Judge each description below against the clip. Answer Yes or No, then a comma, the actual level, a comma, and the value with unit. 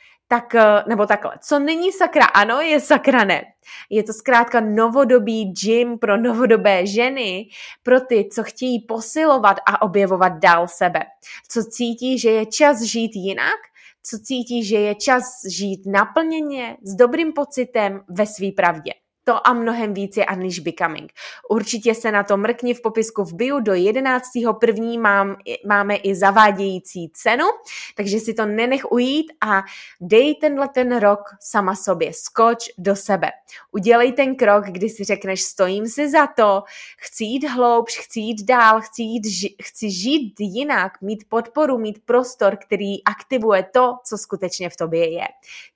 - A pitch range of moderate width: Yes, average, 3.9 semitones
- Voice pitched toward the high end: Yes, high, 225 Hz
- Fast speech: No, average, 155 wpm